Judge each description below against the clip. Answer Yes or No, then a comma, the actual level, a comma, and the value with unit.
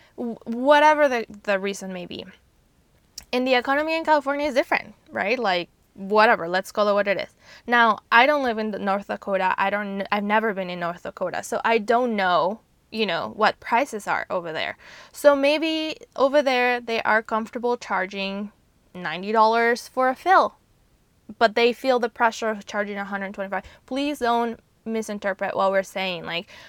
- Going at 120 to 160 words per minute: No, average, 175 wpm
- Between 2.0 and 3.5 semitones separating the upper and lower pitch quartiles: No, average, 4.0 semitones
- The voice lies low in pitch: No, high, 225 Hz